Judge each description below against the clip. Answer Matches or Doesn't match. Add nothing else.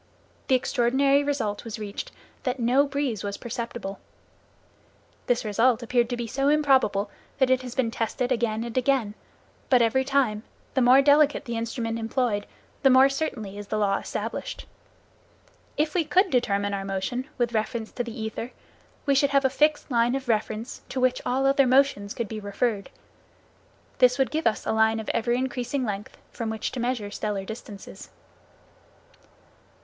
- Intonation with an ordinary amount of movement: Matches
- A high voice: Matches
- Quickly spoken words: Doesn't match